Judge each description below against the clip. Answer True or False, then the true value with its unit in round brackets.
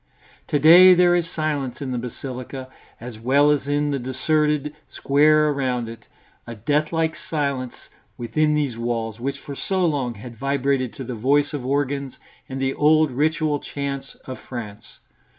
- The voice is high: False (140 Hz)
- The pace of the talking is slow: False (160 wpm)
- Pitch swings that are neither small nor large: True (3.0 semitones)